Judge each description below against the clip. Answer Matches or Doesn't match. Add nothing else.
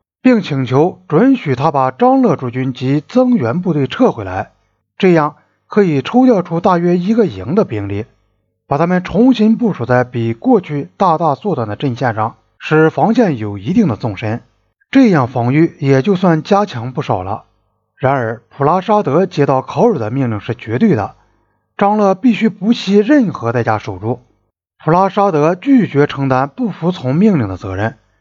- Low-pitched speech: Doesn't match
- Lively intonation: Matches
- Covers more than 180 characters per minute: Matches